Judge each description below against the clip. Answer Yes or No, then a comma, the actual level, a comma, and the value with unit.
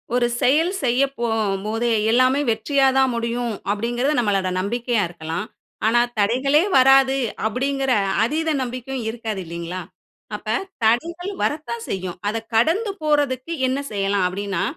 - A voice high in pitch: Yes, high, 240 Hz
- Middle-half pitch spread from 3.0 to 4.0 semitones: No, average, 4.4 semitones